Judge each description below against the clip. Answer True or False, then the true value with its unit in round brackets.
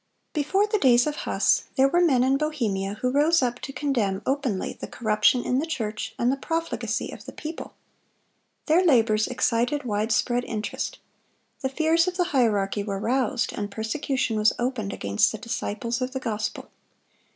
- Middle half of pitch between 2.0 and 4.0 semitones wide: False (5.1 semitones)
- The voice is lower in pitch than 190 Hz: False (250 Hz)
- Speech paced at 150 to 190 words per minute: True (170 wpm)